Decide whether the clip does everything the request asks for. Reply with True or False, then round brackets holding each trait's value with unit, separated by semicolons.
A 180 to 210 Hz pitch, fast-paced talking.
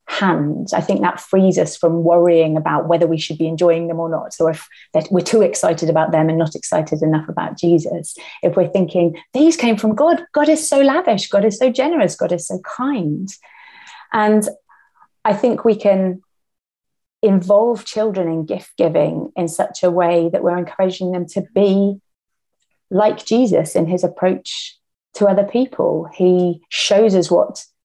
False (190 Hz; 175 wpm)